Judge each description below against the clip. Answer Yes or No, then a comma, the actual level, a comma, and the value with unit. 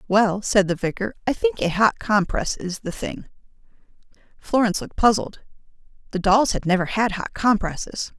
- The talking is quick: No, average, 160 wpm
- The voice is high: Yes, high, 210 Hz